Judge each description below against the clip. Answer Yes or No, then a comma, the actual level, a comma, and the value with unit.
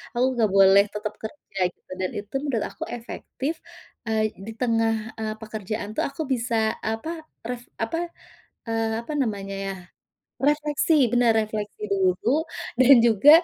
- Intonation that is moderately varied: Yes, average, 3.3 semitones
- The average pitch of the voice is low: No, high, 225 Hz